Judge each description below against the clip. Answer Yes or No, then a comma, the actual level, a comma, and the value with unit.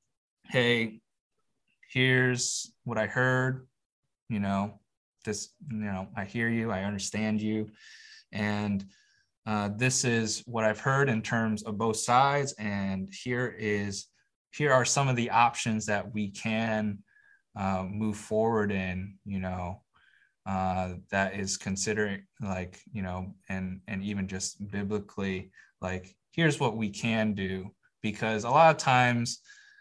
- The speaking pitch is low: Yes, low, 110 Hz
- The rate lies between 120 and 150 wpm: Yes, average, 140 wpm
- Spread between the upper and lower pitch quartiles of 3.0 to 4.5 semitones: Yes, average, 3.5 semitones